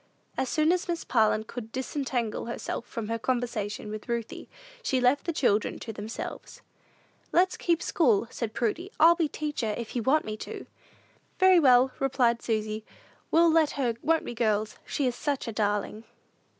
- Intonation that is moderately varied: No, wide, 5.7 semitones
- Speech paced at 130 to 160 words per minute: No, average, 170 wpm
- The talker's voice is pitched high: Yes, high, 245 Hz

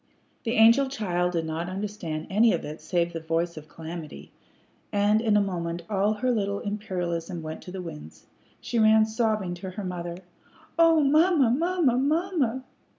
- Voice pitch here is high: Yes, high, 200 Hz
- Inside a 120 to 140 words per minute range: No, average, 165 wpm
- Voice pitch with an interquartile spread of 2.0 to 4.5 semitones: No, average, 5.2 semitones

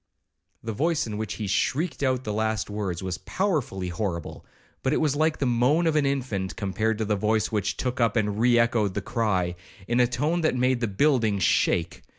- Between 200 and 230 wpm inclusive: Yes, fast, 205 wpm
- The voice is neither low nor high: No, low, 115 Hz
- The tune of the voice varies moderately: Yes, average, 4.2 semitones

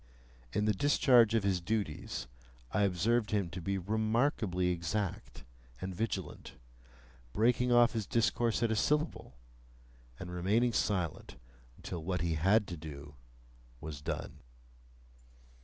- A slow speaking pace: Yes, slow, 125 wpm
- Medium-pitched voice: No, low, 100 Hz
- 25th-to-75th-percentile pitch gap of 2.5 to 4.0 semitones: No, average, 4.5 semitones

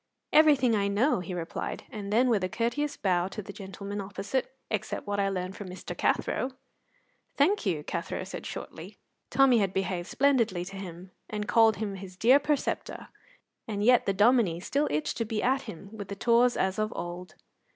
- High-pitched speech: Yes, high, 205 Hz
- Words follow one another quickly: No, average, 185 wpm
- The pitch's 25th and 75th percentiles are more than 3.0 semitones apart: Yes, average, 4.2 semitones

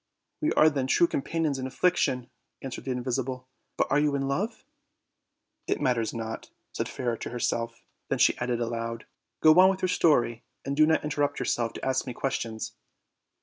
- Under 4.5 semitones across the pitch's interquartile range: Yes, average, 4.1 semitones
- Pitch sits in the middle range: No, low, 130 Hz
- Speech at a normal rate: Yes, average, 185 wpm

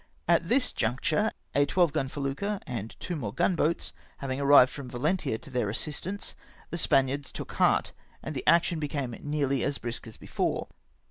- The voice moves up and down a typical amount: Yes, average, 4.3 semitones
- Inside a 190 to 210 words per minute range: No, average, 175 wpm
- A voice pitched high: No, medium, 140 Hz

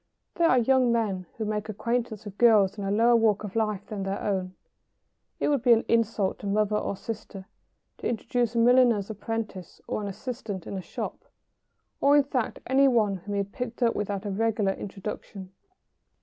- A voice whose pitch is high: Yes, high, 215 Hz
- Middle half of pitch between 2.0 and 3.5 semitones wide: Yes, average, 2.9 semitones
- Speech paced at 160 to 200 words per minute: Yes, average, 190 wpm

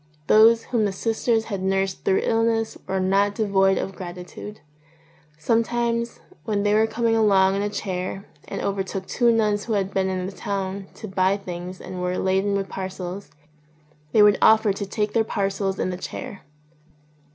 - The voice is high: Yes, high, 200 Hz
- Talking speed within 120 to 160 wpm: No, average, 175 wpm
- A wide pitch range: No, narrow, 2.5 semitones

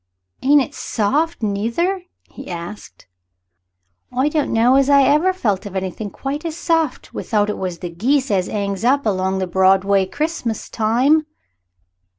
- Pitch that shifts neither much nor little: No, wide, 6.8 semitones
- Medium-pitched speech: No, high, 230 Hz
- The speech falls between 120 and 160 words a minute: Yes, average, 155 wpm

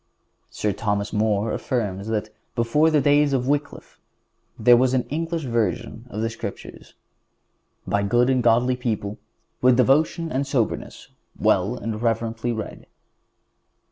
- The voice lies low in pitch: Yes, low, 120 Hz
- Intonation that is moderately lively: Yes, average, 3.3 semitones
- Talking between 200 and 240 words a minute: No, slow, 135 wpm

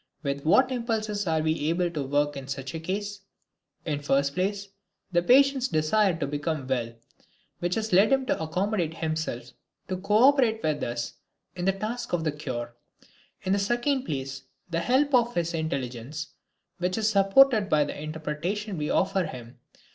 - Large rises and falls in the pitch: Yes, wide, 6.2 semitones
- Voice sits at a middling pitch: Yes, medium, 170 Hz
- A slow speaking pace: No, average, 175 wpm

